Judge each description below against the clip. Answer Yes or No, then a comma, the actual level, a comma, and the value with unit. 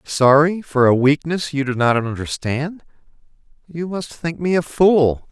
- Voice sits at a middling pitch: Yes, medium, 150 Hz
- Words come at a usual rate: Yes, average, 160 wpm